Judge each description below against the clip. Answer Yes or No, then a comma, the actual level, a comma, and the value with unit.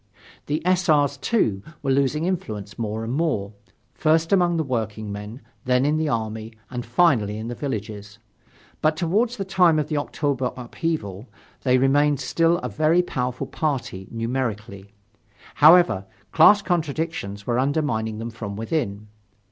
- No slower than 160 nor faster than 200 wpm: No, average, 145 wpm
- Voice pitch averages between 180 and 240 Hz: No, low, 130 Hz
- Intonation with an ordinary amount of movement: No, wide, 6.3 semitones